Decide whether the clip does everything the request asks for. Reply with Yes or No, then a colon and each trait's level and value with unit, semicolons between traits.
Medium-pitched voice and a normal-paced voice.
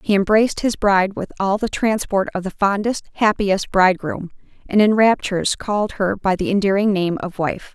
No: high, 200 Hz; average, 185 wpm